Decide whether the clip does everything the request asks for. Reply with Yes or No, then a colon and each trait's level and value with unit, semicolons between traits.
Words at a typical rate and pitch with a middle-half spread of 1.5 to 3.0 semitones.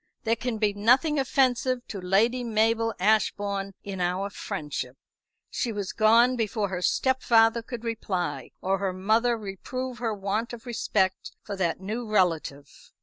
No: average, 145 wpm; average, 3.4 semitones